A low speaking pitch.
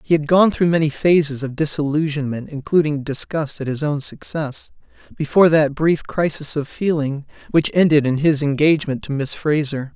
No: medium, 150 Hz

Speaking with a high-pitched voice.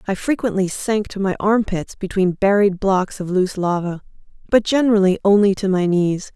Yes: high, 195 Hz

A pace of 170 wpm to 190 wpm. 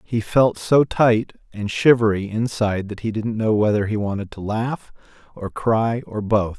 Yes: average, 180 wpm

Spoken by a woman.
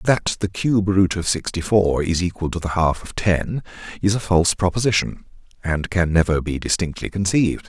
No: male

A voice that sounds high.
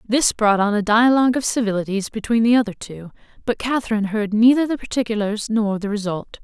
Yes: high, 220 Hz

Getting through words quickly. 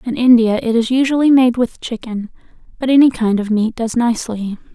No: average, 190 wpm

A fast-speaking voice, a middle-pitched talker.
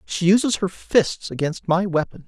No: average, 185 wpm; medium, 180 Hz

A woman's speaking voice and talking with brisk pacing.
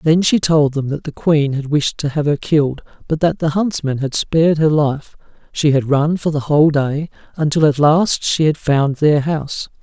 No: male; fast, 220 wpm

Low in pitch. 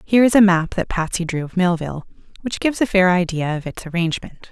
No: medium, 185 Hz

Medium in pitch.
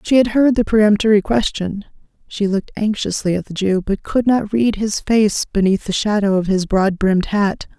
No: high, 205 Hz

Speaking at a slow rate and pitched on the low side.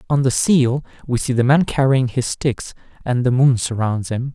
No: fast, 205 wpm; low, 125 Hz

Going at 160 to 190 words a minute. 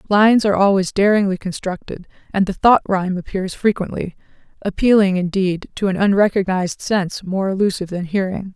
No: average, 140 wpm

